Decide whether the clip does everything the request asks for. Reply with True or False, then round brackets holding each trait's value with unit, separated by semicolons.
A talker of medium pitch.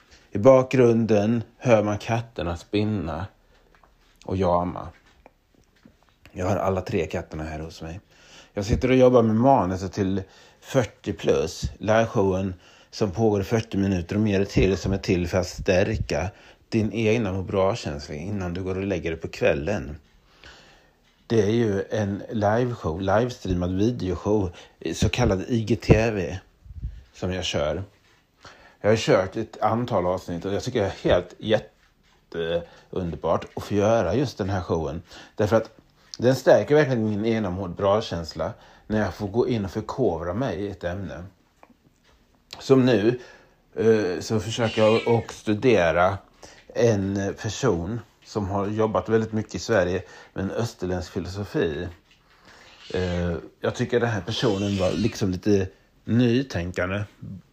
False (100 Hz)